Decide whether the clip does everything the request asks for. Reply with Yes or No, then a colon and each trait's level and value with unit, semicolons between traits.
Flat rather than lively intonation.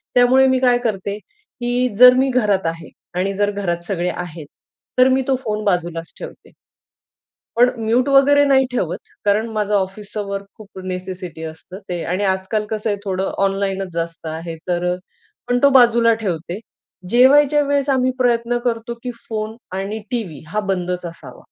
No: average, 5.3 semitones